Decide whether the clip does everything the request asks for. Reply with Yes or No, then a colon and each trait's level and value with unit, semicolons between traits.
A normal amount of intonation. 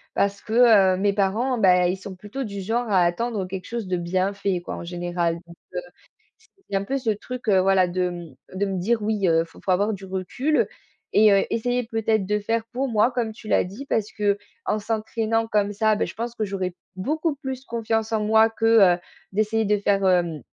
Yes: average, 3.2 semitones